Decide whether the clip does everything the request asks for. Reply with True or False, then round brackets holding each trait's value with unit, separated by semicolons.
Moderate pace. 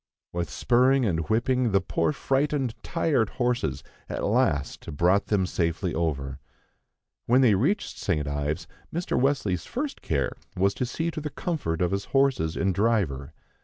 True (155 wpm)